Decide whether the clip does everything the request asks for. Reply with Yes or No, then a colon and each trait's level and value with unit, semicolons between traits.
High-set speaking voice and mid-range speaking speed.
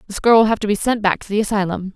No: high, 210 Hz; fast, 335 wpm